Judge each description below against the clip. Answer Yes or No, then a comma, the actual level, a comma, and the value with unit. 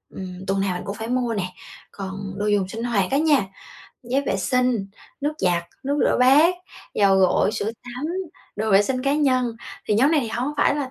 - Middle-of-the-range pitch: No, high, 230 Hz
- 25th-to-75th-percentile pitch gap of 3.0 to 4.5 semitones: No, average, 5.2 semitones